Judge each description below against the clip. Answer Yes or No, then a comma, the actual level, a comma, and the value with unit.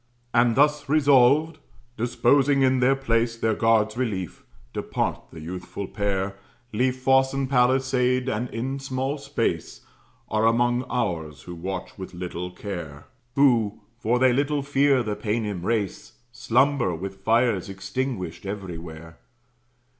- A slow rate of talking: Yes, slow, 130 wpm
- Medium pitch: No, low, 115 Hz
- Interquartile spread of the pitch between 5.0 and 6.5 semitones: Yes, wide, 5.4 semitones